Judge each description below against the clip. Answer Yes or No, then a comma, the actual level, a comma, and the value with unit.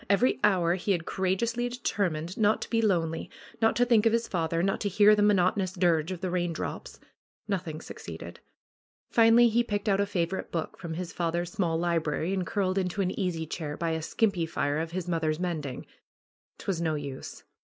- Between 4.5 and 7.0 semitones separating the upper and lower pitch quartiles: No, average, 3.7 semitones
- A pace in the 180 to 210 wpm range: Yes, average, 190 wpm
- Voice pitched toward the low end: No, medium, 180 Hz